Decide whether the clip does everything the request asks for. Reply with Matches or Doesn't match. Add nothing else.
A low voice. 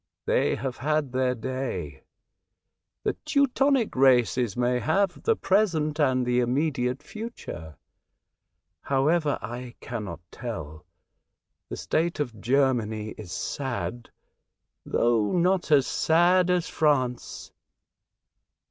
Matches